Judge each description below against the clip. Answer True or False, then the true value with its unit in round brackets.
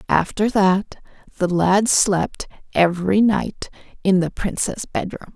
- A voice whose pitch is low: False (190 Hz)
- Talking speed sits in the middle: False (125 wpm)